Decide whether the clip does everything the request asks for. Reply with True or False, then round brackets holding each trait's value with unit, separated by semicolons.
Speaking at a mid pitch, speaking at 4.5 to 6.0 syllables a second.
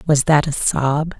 False (150 Hz; 3.9 syllables/s)